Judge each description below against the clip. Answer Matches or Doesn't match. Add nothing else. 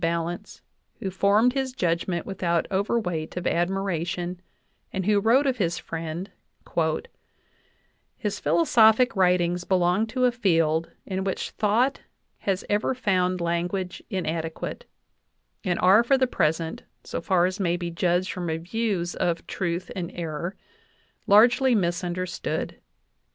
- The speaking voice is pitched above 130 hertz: Matches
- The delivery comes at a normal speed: Doesn't match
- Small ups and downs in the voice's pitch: Doesn't match